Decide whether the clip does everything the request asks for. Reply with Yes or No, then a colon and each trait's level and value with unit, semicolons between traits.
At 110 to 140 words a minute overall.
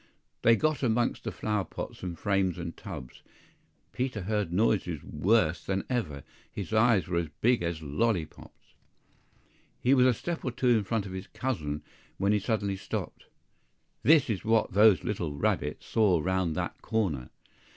No: average, 160 wpm